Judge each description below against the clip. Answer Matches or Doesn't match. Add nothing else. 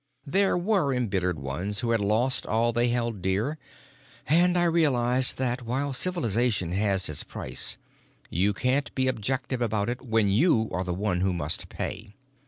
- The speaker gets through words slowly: Doesn't match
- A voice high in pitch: Doesn't match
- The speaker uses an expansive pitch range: Doesn't match